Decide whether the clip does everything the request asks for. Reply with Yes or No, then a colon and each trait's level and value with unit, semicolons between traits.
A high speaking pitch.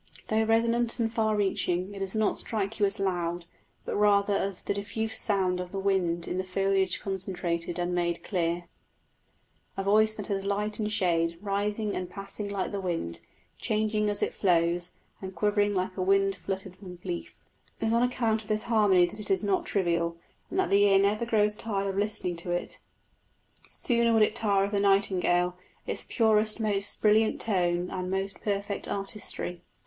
Yes: high, 195 Hz